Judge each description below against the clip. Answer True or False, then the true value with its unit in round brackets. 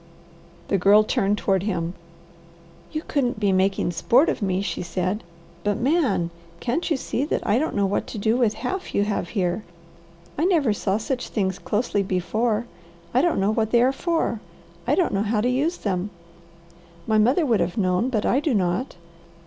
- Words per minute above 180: True (190 wpm)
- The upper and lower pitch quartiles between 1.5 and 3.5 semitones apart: False (4.6 semitones)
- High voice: True (215 Hz)